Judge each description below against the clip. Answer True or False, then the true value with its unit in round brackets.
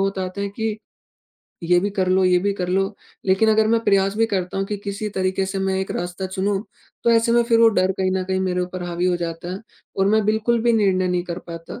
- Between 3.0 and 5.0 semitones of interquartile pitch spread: False (2.5 semitones)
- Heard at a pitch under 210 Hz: True (190 Hz)